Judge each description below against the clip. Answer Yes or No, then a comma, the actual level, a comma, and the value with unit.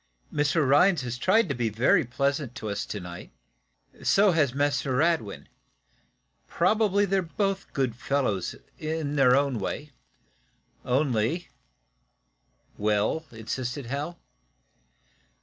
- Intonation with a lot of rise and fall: Yes, wide, 5.7 semitones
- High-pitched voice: No, medium, 140 Hz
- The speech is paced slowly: Yes, slow, 115 wpm